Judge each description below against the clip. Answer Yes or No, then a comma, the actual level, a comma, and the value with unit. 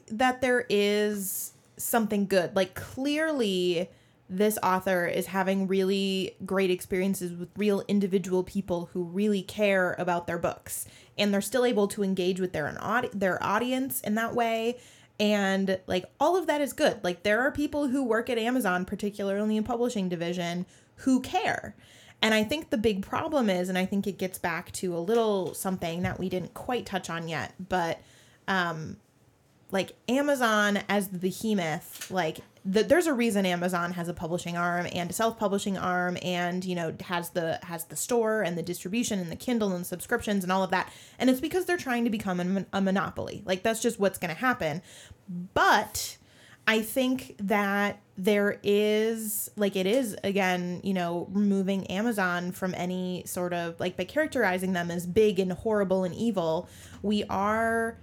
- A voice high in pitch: Yes, high, 195 Hz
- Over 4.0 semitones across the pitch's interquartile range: No, average, 3.6 semitones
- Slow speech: No, average, 180 wpm